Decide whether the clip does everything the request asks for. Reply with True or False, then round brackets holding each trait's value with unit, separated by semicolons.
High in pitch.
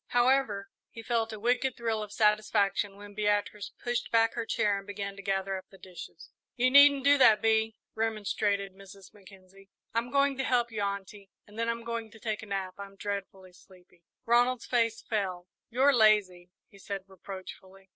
True (210 Hz)